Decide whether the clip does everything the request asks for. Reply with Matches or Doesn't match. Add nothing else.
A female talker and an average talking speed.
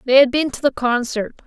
Doesn't match